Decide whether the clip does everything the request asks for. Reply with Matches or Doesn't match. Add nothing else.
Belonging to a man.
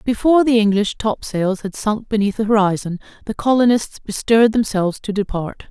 Doesn't match